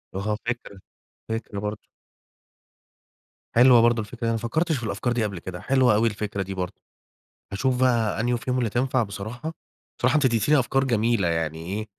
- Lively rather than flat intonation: No, average, 3.6 semitones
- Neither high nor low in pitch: No, low, 115 Hz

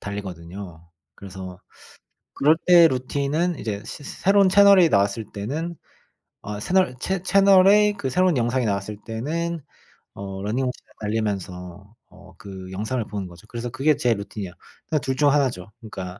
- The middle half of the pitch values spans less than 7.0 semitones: No, wide, 8.0 semitones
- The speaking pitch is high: No, low, 115 Hz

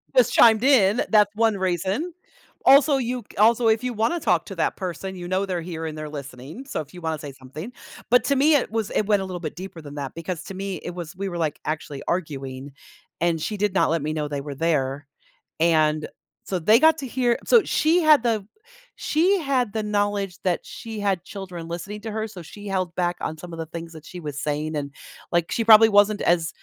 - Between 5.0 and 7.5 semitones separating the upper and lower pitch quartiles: Yes, wide, 5.6 semitones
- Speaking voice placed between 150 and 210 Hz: Yes, medium, 185 Hz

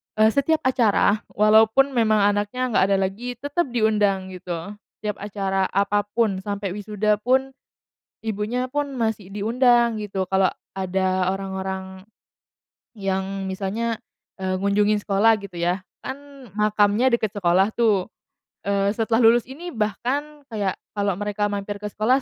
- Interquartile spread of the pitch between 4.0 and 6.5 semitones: No, average, 3.2 semitones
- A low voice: No, high, 210 Hz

